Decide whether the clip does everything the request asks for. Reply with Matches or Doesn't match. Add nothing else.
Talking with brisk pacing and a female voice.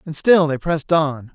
Doesn't match